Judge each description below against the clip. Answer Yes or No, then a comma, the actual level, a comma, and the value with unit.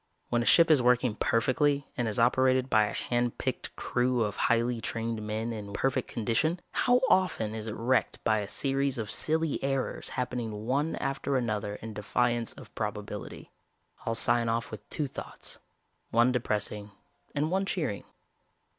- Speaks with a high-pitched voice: No, low, 120 Hz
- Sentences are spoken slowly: No, average, 165 wpm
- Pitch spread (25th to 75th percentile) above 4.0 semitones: No, average, 3.5 semitones